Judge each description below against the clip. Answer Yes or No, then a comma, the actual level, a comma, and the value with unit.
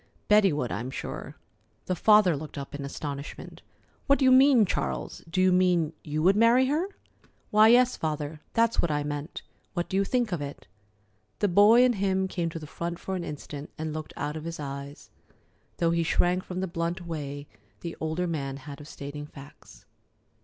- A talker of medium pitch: Yes, medium, 170 Hz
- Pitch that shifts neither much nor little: Yes, average, 4.8 semitones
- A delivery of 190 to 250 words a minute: Yes, average, 195 wpm